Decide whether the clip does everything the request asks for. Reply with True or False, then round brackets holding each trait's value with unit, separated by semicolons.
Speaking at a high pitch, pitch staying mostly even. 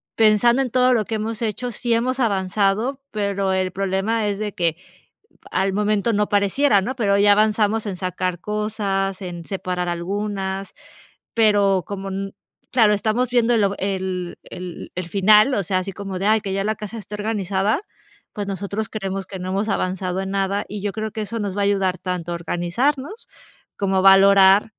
True (200 Hz; 2.2 semitones)